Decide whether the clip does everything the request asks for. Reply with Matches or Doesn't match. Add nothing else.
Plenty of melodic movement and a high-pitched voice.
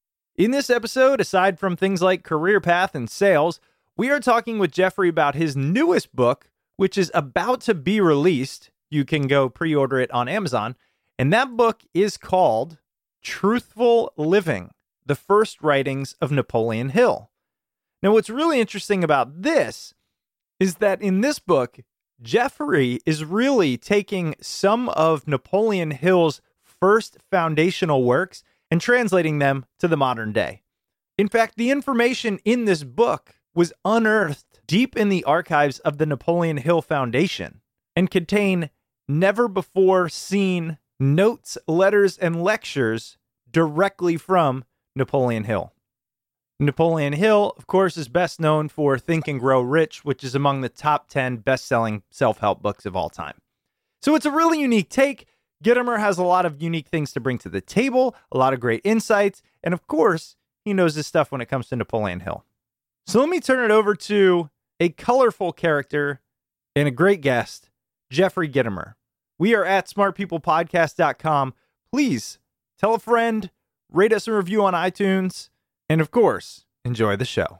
Doesn't match